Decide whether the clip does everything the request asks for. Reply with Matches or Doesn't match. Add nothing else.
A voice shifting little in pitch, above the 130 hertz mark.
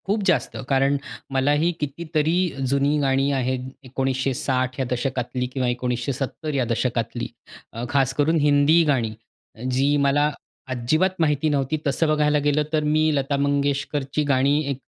Matches